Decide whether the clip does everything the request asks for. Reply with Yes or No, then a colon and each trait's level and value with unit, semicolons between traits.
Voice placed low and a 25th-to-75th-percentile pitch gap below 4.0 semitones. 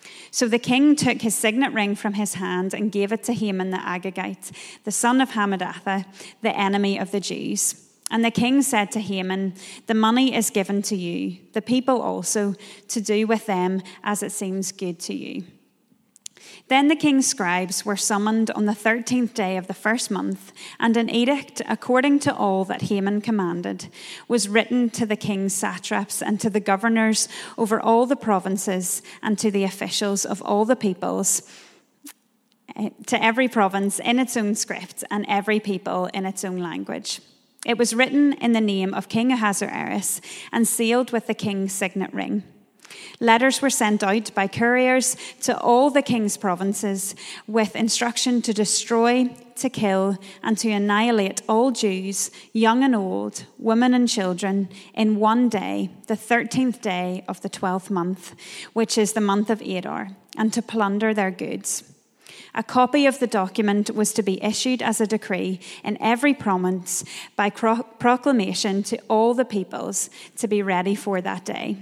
No: high, 215 Hz; average, 3.1 semitones